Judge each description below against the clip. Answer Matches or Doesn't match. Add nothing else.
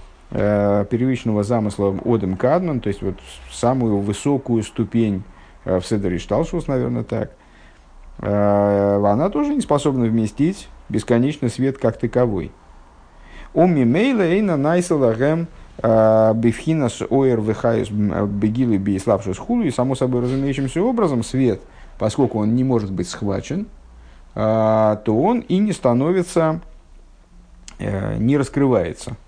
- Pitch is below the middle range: Matches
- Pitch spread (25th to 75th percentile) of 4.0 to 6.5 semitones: Matches